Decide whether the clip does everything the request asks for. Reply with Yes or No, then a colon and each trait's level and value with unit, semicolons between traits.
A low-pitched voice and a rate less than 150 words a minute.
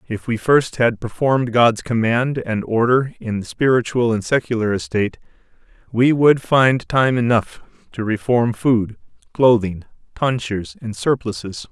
Yes: low, 115 Hz; average, 140 wpm